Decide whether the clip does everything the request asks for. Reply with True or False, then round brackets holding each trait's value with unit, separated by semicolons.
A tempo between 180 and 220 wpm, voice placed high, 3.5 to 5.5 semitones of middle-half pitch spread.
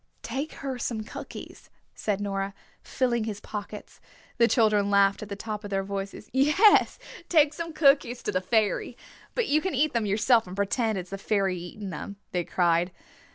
True (185 wpm; 210 Hz; 4.3 semitones)